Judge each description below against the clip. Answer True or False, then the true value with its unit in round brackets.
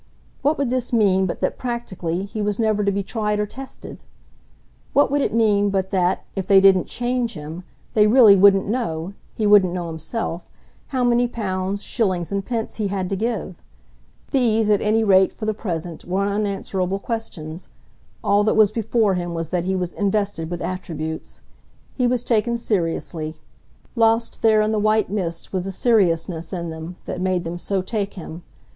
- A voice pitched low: False (200 Hz)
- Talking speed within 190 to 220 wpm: False (180 wpm)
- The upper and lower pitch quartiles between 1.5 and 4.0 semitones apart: True (3.6 semitones)